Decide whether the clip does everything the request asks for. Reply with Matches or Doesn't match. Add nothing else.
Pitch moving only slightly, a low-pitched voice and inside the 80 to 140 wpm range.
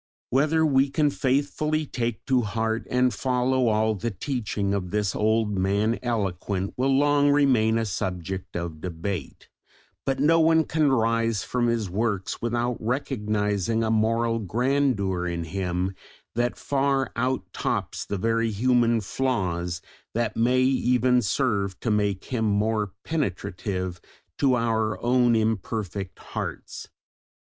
Doesn't match